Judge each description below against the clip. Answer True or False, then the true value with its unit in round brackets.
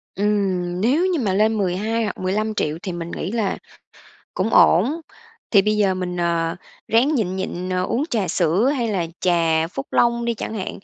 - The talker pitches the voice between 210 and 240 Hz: False (195 Hz)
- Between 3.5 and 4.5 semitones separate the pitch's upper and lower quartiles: True (3.9 semitones)